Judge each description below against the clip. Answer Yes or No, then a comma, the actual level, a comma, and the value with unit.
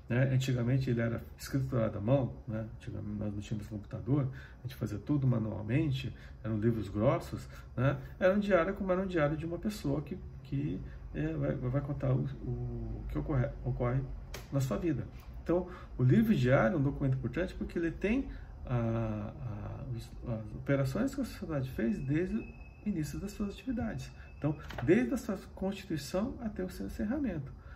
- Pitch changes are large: Yes, wide, 6.7 semitones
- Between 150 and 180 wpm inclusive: Yes, average, 175 wpm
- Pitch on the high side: No, low, 135 Hz